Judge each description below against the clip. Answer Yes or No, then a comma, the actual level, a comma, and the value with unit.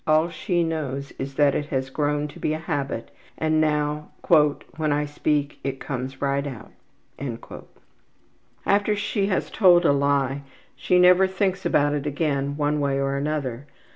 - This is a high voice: No, medium, 145 Hz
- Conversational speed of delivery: Yes, average, 165 wpm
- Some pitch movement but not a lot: No, narrow, 2.3 semitones